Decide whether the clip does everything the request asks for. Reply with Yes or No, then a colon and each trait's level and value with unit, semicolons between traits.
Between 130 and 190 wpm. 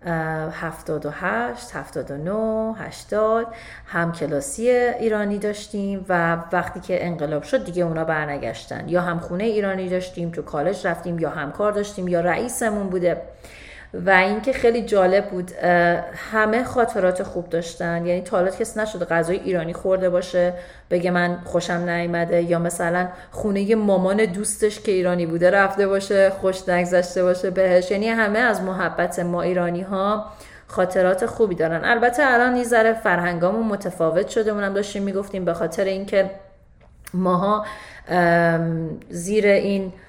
Yes: average, 140 wpm